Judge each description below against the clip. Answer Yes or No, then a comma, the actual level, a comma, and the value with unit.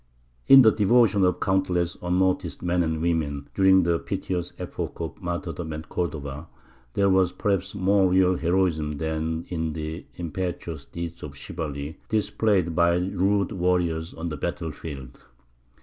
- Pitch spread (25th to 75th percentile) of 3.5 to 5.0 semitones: No, average, 2.9 semitones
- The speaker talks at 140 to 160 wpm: Yes, average, 145 wpm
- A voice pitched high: No, very low, 85 Hz